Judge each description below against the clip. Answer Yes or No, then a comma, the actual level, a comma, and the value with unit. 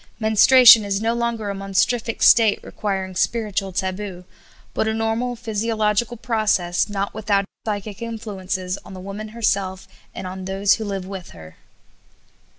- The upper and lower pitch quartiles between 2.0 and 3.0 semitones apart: Yes, narrow, 2.6 semitones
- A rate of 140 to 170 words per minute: Yes, average, 150 wpm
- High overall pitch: Yes, high, 205 Hz